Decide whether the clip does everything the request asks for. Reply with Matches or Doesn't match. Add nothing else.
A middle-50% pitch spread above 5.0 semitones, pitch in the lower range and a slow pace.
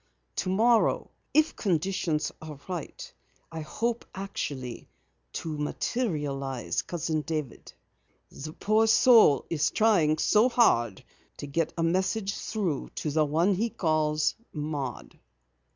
Doesn't match